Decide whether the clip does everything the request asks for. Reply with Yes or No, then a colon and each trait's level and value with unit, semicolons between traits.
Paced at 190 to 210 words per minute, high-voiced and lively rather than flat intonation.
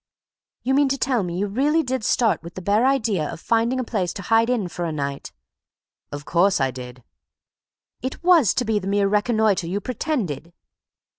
Yes: average, 195 wpm; high, 205 Hz; wide, 6.3 semitones